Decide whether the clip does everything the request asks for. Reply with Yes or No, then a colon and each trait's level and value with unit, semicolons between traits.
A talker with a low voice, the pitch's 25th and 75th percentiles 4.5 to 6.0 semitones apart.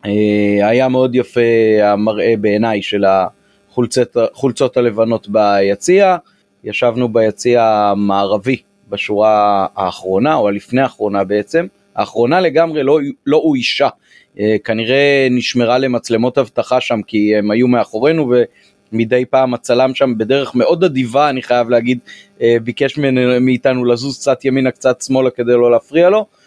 No: low, 120 Hz; average, 3.8 semitones